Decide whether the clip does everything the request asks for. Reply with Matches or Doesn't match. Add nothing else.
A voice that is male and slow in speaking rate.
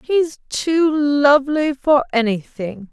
Doesn't match